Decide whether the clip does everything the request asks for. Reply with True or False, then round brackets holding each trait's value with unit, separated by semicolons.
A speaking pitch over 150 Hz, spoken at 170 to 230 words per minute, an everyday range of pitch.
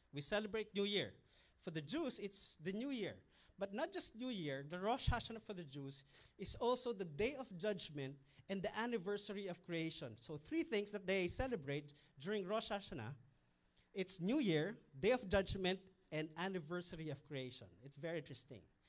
False (185 Hz; 175 wpm; 6.5 semitones)